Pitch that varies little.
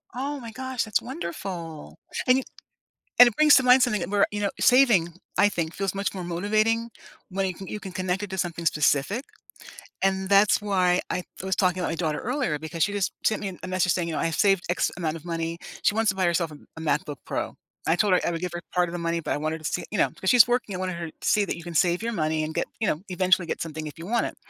No: average, 3.8 semitones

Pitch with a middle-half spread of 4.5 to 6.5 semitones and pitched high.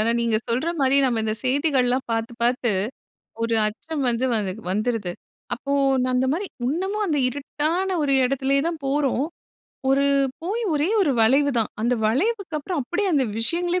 Yes: average, 5.2 semitones; very high, 275 Hz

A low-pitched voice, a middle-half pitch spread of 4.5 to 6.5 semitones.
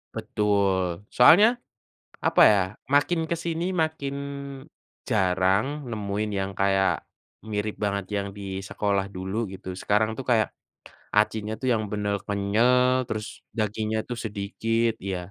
No: low, 105 Hz; average, 3.7 semitones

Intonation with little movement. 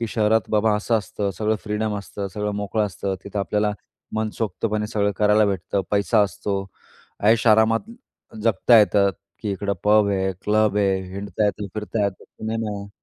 Yes: narrow, 1.3 semitones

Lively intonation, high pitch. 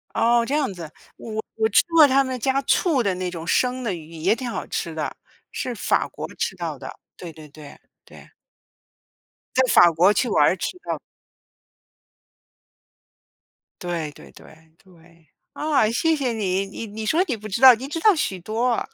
Yes: wide, 6.7 semitones; high, 220 Hz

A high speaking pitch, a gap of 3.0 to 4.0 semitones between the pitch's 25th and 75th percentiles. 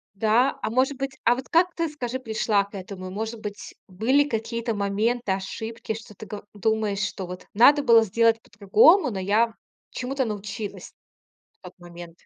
Yes: high, 220 Hz; average, 3.6 semitones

